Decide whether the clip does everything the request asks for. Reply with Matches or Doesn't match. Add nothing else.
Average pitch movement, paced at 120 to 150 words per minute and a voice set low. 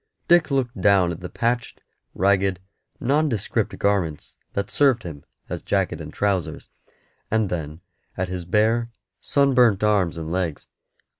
Matches